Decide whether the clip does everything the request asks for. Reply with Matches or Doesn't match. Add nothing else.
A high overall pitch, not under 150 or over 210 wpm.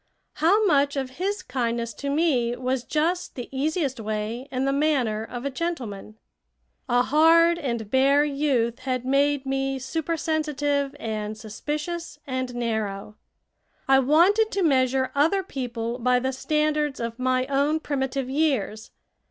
Doesn't match